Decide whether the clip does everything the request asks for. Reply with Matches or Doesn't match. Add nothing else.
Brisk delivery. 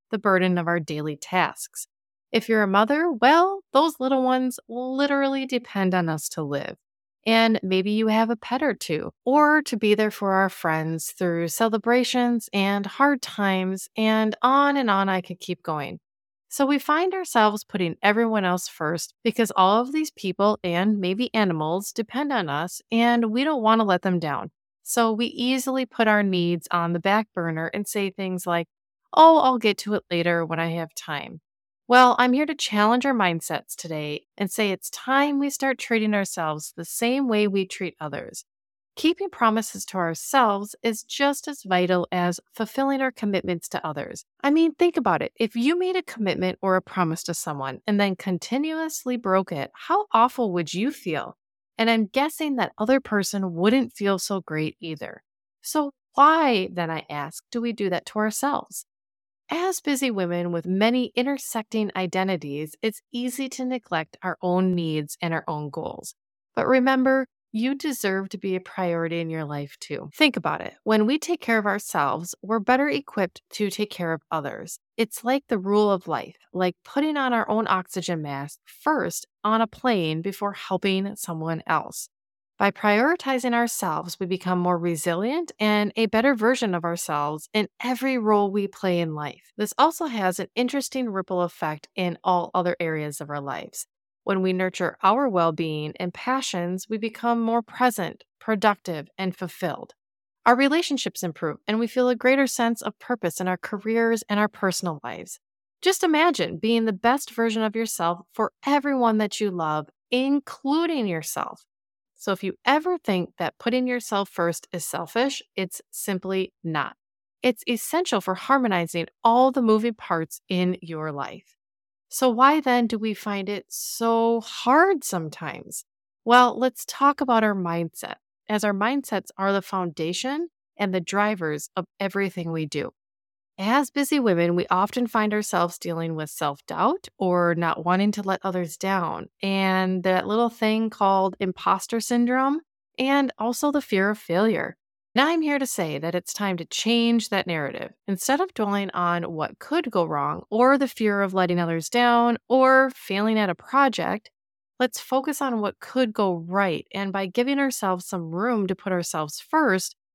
Doesn't match